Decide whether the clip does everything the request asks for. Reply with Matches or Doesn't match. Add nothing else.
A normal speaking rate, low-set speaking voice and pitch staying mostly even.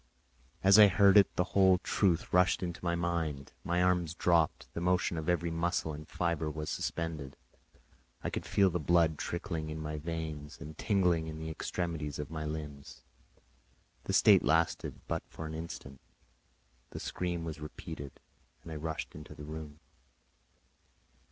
Matches